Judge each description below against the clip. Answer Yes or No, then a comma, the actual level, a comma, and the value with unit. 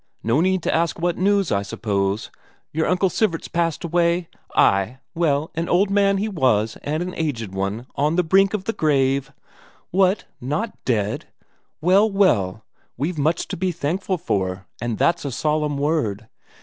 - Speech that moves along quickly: No, average, 165 wpm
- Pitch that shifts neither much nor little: No, wide, 7.2 semitones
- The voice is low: No, medium, 160 Hz